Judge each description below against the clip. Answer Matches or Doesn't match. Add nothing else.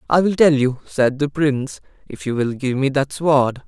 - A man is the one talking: Matches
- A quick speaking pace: Matches